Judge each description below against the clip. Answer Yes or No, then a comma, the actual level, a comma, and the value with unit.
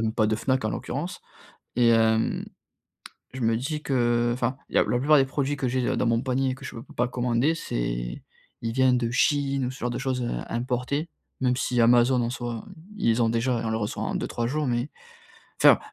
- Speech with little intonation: Yes, narrow, 2.2 semitones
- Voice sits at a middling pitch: No, low, 125 Hz